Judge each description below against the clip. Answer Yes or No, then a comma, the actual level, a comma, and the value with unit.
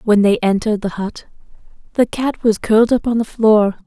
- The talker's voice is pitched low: No, high, 215 Hz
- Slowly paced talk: No, average, 200 wpm